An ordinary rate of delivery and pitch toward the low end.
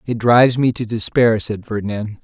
Yes: average, 190 wpm; low, 115 Hz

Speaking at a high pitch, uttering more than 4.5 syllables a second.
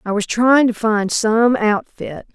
No: high, 220 Hz; 3.7 syllables/s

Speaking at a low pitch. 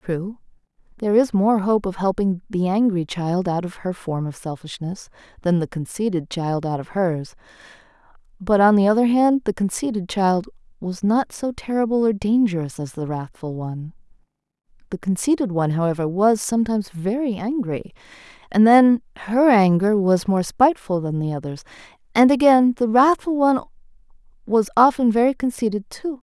No: high, 205 Hz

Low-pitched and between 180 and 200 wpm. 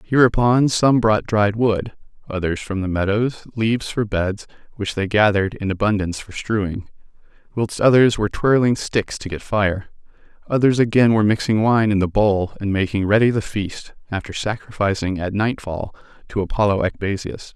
No: low, 105 Hz; average, 160 wpm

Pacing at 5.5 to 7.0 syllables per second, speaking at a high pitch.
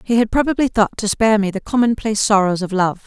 Yes: 6.4 syllables/s; high, 215 Hz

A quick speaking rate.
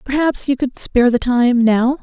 Yes: fast, 210 wpm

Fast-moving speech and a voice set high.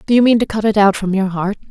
Yes: fast, 350 wpm; high, 205 Hz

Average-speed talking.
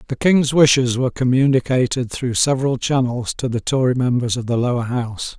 Yes: average, 180 wpm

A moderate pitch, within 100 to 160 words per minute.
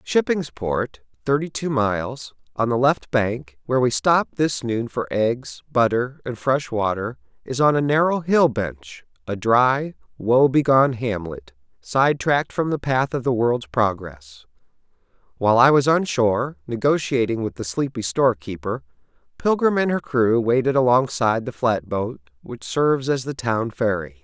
No: low, 120 Hz; average, 155 wpm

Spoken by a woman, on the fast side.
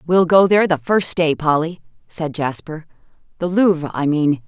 No: female; average, 175 wpm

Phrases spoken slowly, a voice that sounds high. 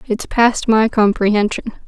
Yes: slow, 130 wpm; high, 220 Hz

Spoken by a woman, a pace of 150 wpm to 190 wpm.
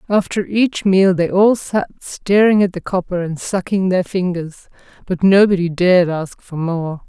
Yes: female; average, 170 wpm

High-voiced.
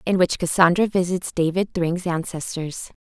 No: medium, 175 Hz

